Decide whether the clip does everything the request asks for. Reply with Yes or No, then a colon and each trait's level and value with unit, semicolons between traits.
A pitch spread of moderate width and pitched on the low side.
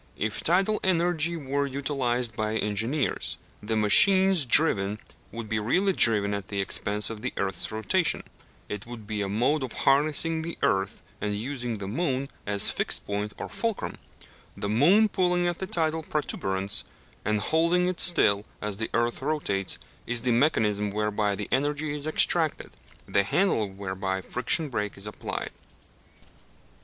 No: wide, 7.2 semitones; low, 120 Hz